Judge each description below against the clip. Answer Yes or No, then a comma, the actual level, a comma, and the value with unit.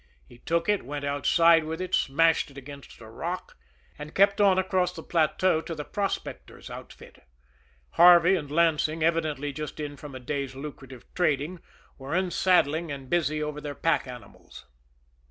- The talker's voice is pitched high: No, medium, 155 Hz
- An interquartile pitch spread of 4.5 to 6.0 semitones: No, average, 3.3 semitones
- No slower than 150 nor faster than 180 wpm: Yes, average, 160 wpm